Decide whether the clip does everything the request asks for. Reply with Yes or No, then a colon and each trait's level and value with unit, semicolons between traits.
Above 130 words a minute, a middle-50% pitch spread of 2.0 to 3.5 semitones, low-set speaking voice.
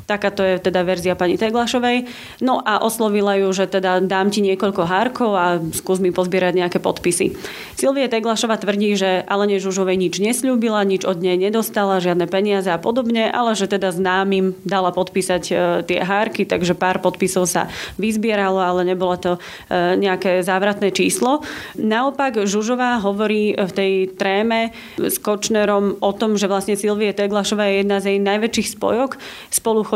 No: average, 160 wpm; narrow, 2.6 semitones; high, 200 Hz